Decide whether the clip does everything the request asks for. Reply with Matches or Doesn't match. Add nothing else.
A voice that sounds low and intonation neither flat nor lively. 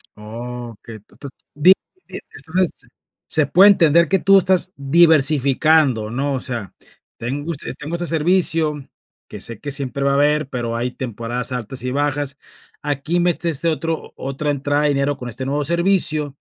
Doesn't match